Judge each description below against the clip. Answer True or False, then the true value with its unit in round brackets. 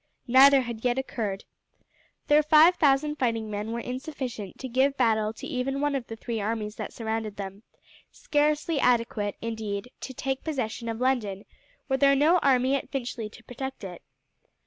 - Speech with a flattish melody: False (3.8 semitones)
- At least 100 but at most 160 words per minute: False (170 wpm)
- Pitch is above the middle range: True (250 Hz)